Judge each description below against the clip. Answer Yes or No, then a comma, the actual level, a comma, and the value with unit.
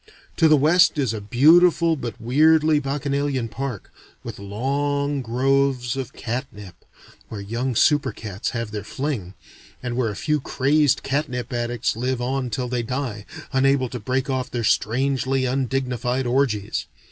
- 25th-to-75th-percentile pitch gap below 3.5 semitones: Yes, average, 2.9 semitones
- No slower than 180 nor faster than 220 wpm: No, average, 145 wpm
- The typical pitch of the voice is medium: No, low, 130 Hz